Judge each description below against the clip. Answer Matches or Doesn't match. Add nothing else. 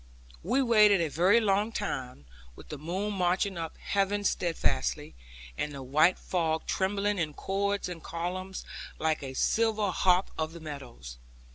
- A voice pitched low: Doesn't match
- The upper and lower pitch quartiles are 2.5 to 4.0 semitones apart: Doesn't match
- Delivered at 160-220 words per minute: Doesn't match